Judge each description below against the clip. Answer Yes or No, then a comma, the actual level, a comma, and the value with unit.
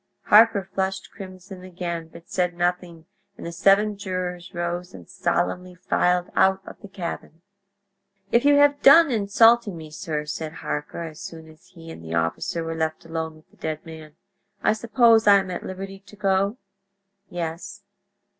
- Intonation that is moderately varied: Yes, average, 3.4 semitones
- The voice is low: No, medium, 180 Hz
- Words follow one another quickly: No, average, 165 wpm